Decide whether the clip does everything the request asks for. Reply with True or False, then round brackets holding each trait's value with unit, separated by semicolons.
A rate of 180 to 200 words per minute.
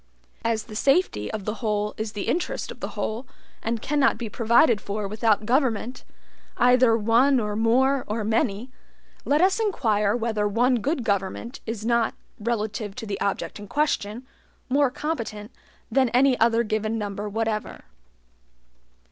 False (150 wpm)